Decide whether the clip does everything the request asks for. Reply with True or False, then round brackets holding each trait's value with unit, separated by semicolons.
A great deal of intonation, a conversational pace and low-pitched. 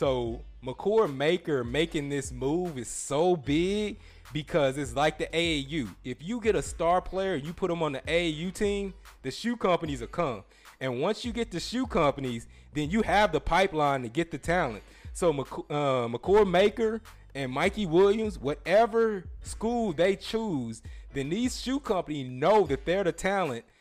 False (6.7 semitones; 175 wpm; 170 Hz)